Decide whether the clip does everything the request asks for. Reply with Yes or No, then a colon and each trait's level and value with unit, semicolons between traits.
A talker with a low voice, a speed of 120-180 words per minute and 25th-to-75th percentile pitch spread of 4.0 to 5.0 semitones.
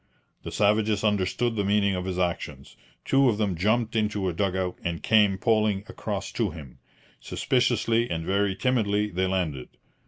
No: low, 100 Hz; average, 165 wpm; average, 2.9 semitones